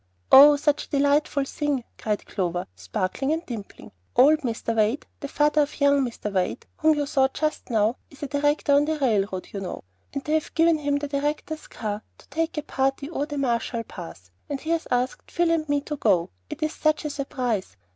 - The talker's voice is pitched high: Yes, very high, 280 Hz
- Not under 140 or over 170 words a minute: No, fast, 205 wpm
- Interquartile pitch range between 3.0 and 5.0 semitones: Yes, average, 4.6 semitones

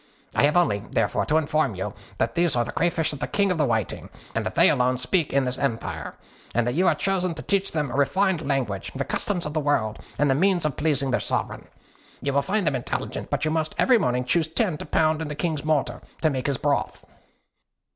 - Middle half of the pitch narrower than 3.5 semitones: No, average, 4.6 semitones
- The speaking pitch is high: No, medium, 150 Hz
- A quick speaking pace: Yes, fast, 230 wpm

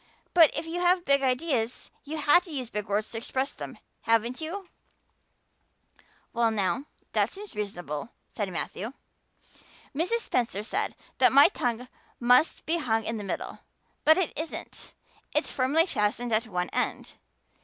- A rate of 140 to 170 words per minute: Yes, average, 155 wpm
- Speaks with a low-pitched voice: No, very high, 250 Hz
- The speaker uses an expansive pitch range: Yes, wide, 6.3 semitones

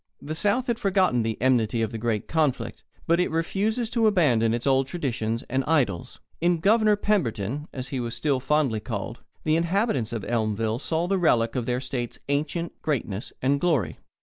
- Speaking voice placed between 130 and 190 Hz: Yes, low, 135 Hz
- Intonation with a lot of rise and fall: Yes, wide, 6.7 semitones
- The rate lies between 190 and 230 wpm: No, average, 180 wpm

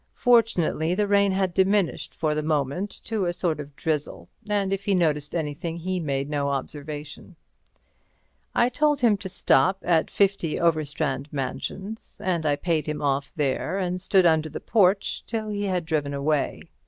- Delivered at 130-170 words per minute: Yes, average, 165 wpm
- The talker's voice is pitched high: No, medium, 170 Hz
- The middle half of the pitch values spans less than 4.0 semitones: No, average, 4.7 semitones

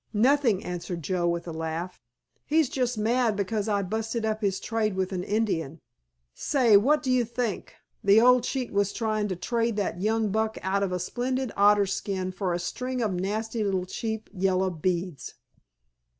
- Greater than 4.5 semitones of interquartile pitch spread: No, average, 3.6 semitones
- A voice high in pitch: Yes, high, 205 Hz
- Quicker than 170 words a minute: Yes, average, 180 wpm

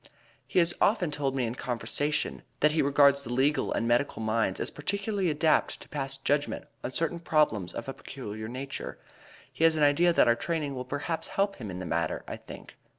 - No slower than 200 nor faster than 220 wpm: Yes, fast, 205 wpm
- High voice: No, medium, 140 Hz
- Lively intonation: No, average, 4.8 semitones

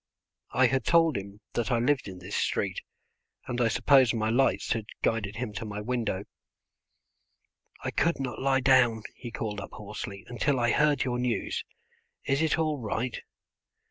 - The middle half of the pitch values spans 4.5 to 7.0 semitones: No, average, 3.8 semitones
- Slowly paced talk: No, average, 170 wpm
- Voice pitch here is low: Yes, low, 120 Hz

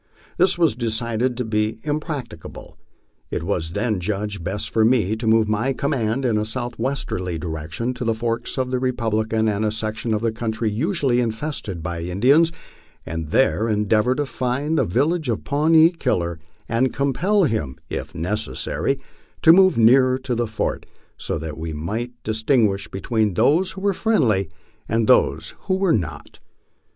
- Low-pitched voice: Yes, low, 115 Hz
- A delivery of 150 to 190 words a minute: Yes, average, 160 wpm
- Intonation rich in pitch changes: No, average, 4.1 semitones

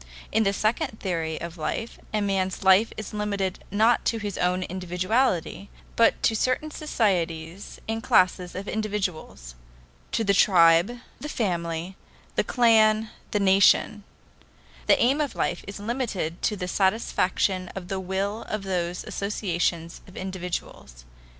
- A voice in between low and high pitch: No, high, 195 Hz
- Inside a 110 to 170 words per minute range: Yes, average, 140 wpm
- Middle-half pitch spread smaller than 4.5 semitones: Yes, average, 3.3 semitones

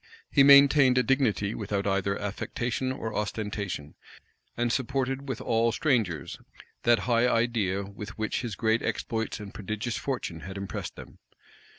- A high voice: No, low, 115 Hz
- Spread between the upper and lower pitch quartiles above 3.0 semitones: Yes, average, 3.9 semitones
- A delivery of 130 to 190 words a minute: Yes, average, 145 wpm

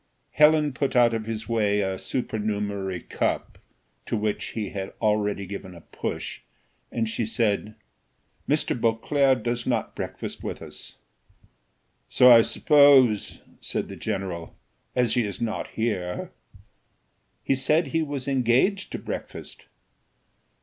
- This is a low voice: Yes, low, 115 Hz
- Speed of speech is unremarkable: No, slow, 130 wpm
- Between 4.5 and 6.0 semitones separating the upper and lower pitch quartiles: No, average, 4.0 semitones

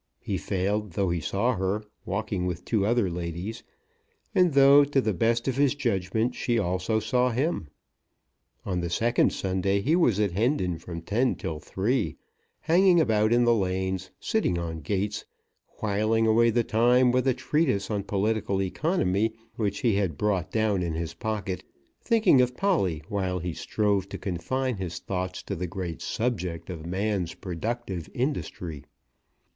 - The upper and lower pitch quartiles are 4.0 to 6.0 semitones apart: Yes, average, 4.8 semitones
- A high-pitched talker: No, low, 105 Hz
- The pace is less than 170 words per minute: Yes, average, 160 wpm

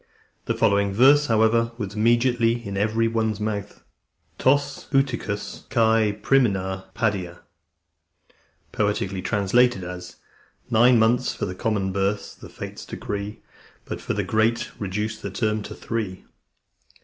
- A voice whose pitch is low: Yes, low, 110 Hz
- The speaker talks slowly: Yes, slow, 115 wpm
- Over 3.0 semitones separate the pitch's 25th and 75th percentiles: No, narrow, 2.6 semitones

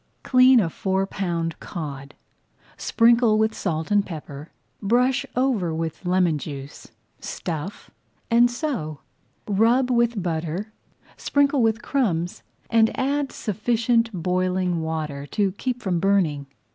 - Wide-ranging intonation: Yes, wide, 6.3 semitones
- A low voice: No, high, 195 Hz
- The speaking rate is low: Yes, slow, 120 wpm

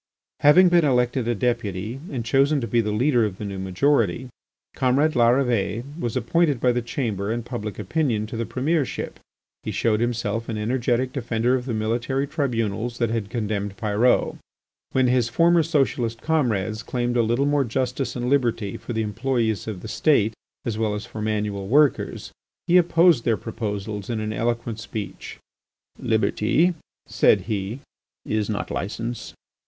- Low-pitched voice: Yes, low, 120 Hz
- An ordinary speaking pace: Yes, average, 160 wpm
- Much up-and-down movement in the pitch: No, average, 3.3 semitones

